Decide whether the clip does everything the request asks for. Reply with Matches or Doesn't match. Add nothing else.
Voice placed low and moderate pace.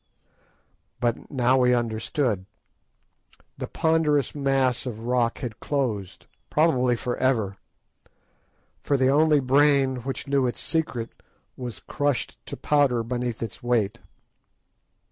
Doesn't match